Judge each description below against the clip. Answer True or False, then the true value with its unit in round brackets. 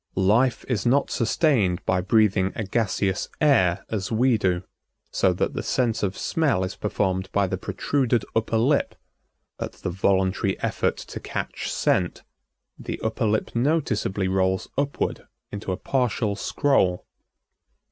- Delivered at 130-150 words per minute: True (140 wpm)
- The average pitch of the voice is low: True (105 Hz)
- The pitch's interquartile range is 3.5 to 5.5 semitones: True (4.4 semitones)